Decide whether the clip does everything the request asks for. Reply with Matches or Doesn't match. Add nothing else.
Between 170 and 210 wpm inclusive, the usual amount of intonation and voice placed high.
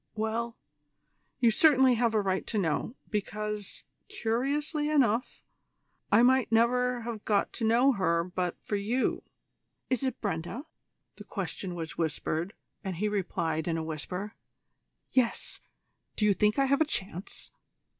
Doesn't match